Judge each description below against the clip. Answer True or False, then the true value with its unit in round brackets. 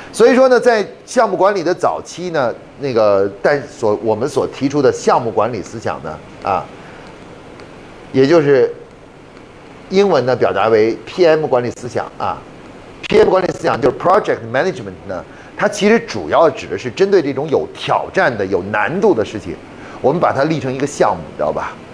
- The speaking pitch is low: False (185 Hz)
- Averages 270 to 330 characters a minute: True (300 characters per minute)